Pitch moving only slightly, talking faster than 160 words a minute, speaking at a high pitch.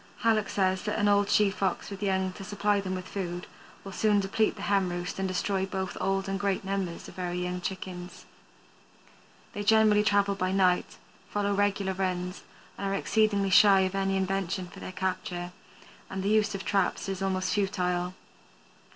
Yes: narrow, 1.5 semitones; average, 180 wpm; high, 195 Hz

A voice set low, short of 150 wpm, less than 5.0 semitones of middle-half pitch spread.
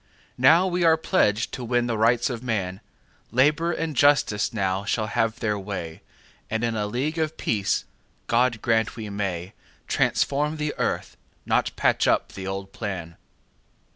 Yes: low, 115 Hz; average, 140 wpm; average, 4.6 semitones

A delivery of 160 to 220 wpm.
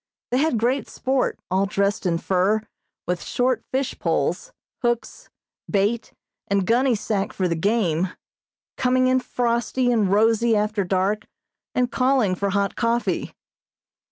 No: slow, 135 wpm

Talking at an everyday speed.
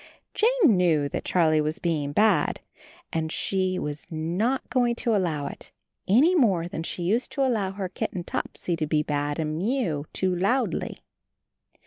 Yes: average, 160 wpm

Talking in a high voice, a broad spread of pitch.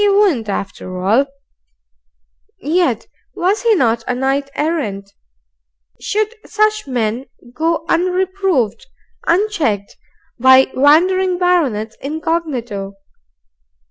Yes: very high, 295 Hz; wide, 7.9 semitones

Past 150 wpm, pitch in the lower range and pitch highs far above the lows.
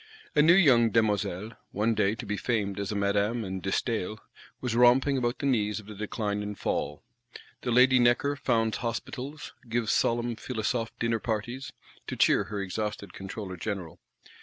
No: average, 170 wpm; low, 110 Hz; average, 2.9 semitones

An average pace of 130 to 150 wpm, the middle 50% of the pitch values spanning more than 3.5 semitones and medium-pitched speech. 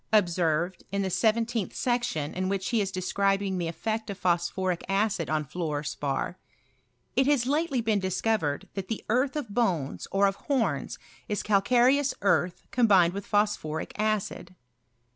No: average, 145 wpm; average, 4.2 semitones; high, 200 Hz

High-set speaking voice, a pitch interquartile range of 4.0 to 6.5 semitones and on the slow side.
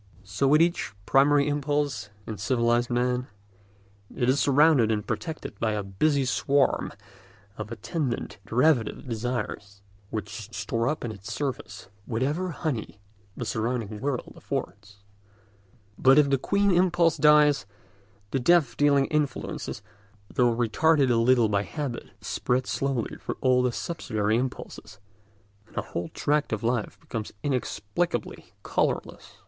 No: low, 125 Hz; average, 4.7 semitones; slow, 130 wpm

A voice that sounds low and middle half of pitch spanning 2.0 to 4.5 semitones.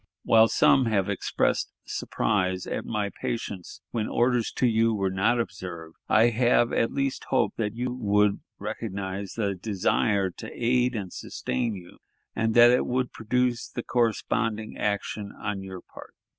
Yes: low, 110 Hz; average, 3.2 semitones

